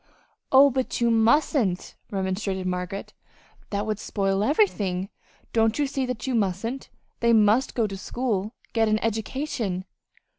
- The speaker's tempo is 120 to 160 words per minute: Yes, average, 140 wpm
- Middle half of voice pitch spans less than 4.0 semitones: No, average, 4.4 semitones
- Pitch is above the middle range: Yes, high, 220 Hz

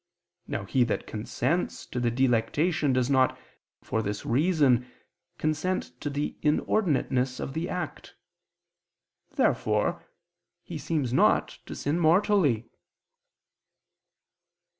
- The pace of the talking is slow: Yes, slow, 105 wpm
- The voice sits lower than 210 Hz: Yes, medium, 140 Hz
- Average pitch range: Yes, average, 4.5 semitones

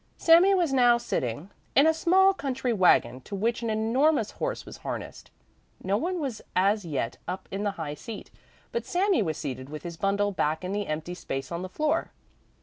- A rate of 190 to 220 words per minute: Yes, average, 195 wpm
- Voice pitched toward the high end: Yes, high, 210 Hz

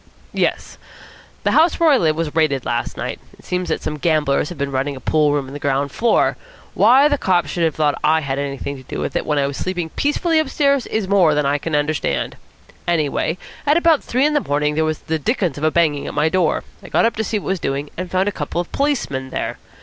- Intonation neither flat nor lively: No, wide, 6.0 semitones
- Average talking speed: No, fast, 250 wpm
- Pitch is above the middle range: No, medium, 160 Hz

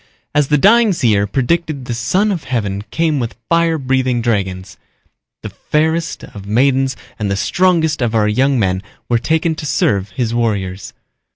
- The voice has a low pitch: Yes, low, 130 Hz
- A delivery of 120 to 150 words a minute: No, average, 165 wpm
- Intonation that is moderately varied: No, wide, 7.0 semitones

